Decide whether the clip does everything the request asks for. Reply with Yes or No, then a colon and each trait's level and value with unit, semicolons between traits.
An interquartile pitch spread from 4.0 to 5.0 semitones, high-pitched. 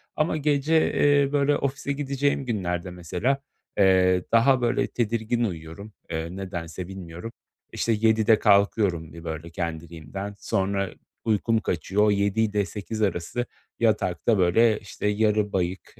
No: average, 4.6 semitones; low, 105 Hz